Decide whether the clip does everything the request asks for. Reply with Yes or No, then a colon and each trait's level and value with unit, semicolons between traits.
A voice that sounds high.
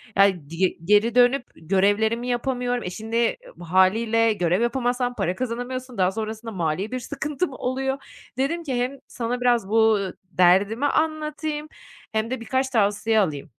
Yes: high, 230 Hz